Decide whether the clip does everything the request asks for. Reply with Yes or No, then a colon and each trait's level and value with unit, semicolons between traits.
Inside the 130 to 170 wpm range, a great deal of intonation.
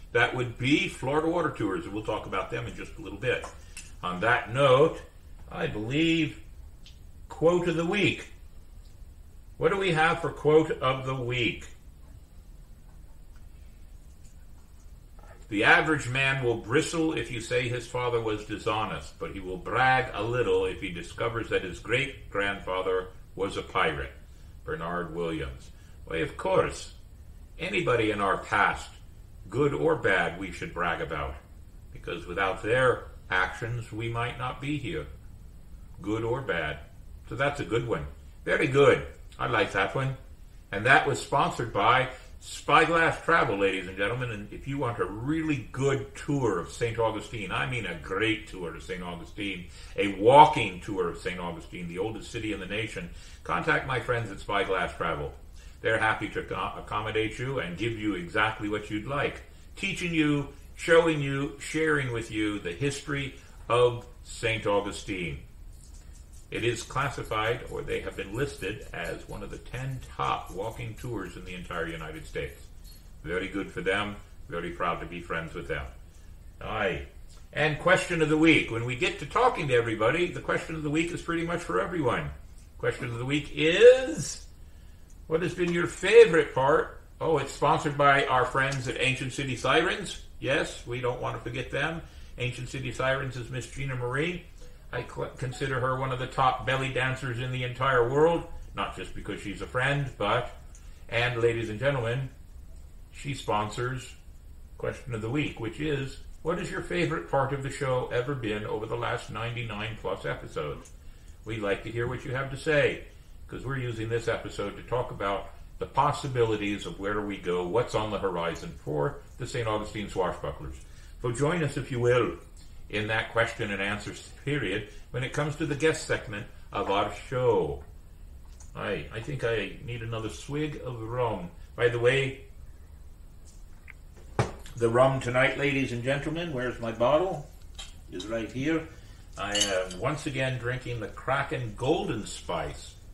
Yes: average, 165 wpm; wide, 7.9 semitones